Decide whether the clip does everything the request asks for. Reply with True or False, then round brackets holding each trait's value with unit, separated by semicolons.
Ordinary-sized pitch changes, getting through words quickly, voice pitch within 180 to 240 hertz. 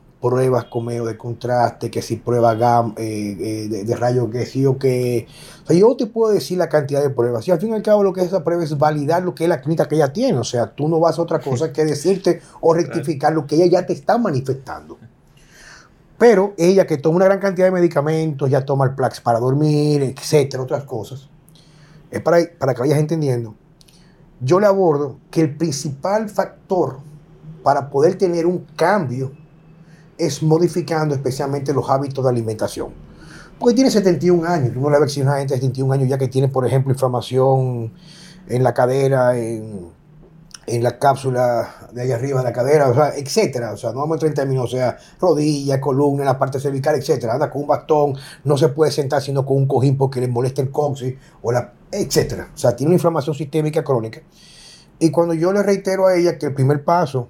False (4.3 semitones; 210 wpm; 145 Hz)